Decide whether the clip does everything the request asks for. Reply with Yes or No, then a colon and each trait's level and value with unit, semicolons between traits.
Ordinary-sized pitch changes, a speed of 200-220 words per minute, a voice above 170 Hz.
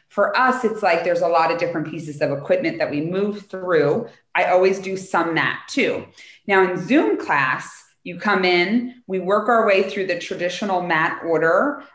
No: average, 3.2 semitones; average, 190 wpm; high, 190 Hz